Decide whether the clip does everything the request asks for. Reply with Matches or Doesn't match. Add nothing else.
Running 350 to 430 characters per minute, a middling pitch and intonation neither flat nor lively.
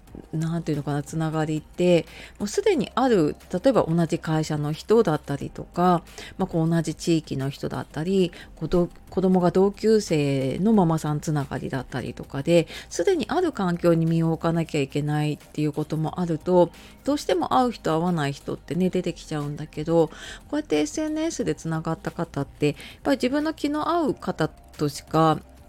Matches